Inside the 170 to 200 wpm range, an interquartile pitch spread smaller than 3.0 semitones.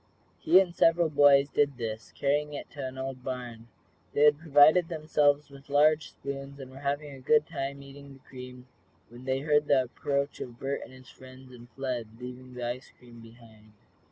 Yes: average, 185 wpm; narrow, 2.4 semitones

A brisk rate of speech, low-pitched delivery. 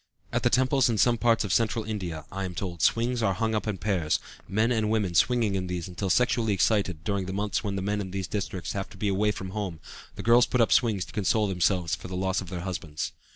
Yes: fast, 250 wpm; low, 100 Hz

